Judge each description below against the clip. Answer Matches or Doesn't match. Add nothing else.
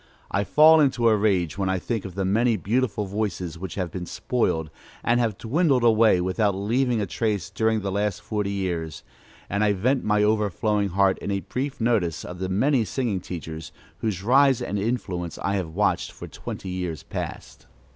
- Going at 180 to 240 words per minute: Matches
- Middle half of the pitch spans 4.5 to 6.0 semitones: Doesn't match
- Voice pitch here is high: Doesn't match